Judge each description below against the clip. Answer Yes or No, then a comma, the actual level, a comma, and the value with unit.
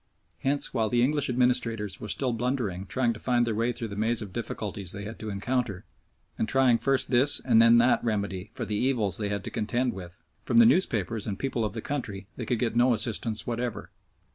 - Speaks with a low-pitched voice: Yes, low, 115 Hz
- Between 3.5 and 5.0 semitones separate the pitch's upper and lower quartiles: No, average, 3.0 semitones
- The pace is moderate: No, fast, 215 wpm